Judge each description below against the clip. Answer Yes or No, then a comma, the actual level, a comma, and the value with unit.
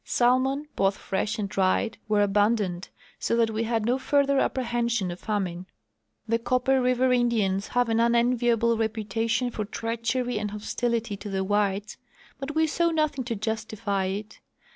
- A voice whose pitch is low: No, high, 225 Hz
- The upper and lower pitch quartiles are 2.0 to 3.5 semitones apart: Yes, average, 3.1 semitones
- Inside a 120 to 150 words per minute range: No, average, 160 wpm